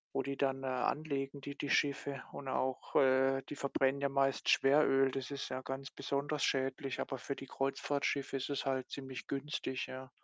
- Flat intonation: Yes, narrow, 0.9 semitones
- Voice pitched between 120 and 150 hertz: Yes, low, 135 Hz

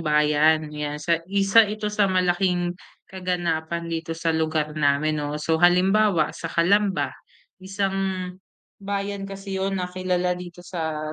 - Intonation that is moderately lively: Yes, average, 3.5 semitones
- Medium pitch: Yes, medium, 175 Hz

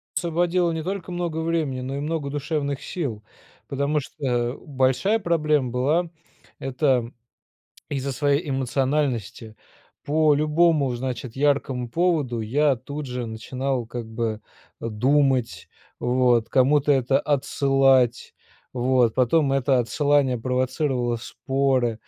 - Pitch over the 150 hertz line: No, low, 135 Hz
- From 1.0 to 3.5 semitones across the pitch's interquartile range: Yes, average, 3.2 semitones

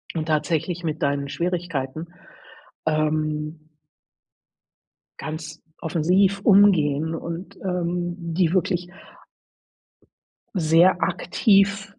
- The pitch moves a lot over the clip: No, average, 2.7 semitones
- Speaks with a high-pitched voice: No, medium, 170 Hz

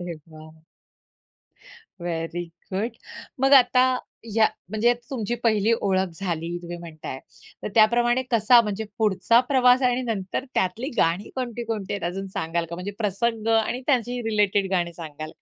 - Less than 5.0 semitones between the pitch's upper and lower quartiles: No, average, 5.3 semitones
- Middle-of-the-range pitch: No, high, 210 Hz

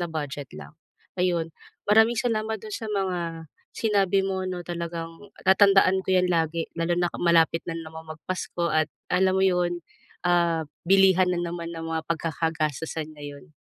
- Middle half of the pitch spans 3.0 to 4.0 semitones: No, narrow, 2.6 semitones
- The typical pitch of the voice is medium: Yes, medium, 175 Hz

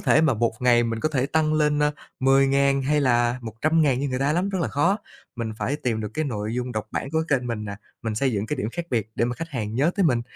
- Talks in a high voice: No, low, 130 Hz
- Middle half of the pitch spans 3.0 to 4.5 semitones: Yes, average, 4.2 semitones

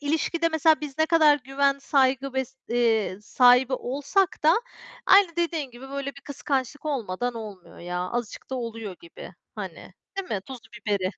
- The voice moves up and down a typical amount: Yes, average, 4.2 semitones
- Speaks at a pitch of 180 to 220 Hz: No, very high, 270 Hz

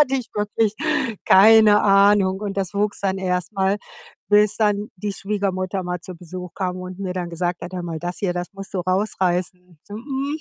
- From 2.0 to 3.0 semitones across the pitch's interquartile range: Yes, narrow, 2.4 semitones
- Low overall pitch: No, high, 190 Hz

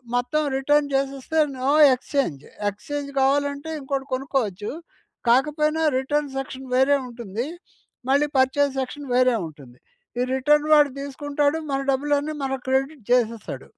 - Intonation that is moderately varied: No, narrow, 2.2 semitones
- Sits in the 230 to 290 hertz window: Yes, very high, 270 Hz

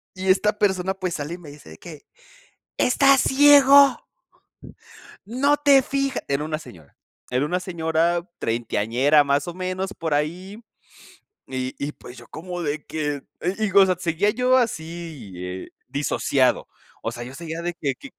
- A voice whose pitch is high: No, medium, 170 Hz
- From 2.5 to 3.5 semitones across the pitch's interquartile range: No, wide, 5.5 semitones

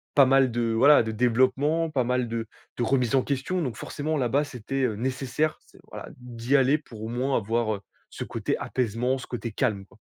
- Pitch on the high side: No, low, 125 Hz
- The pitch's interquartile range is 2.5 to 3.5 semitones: Yes, average, 2.8 semitones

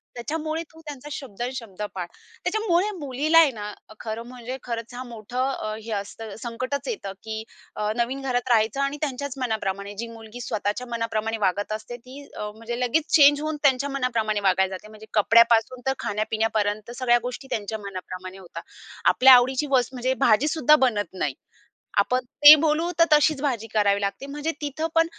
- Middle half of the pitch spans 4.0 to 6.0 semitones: Yes, average, 4.4 semitones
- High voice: Yes, high, 240 Hz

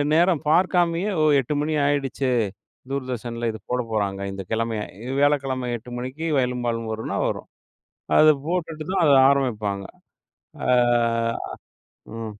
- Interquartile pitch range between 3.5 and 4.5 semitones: No, average, 4.9 semitones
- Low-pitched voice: Yes, low, 130 Hz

